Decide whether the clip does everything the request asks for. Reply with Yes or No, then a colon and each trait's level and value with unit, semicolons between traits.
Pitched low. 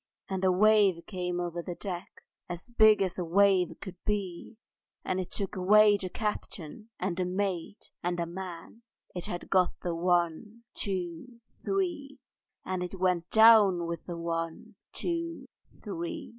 No: medium, 185 Hz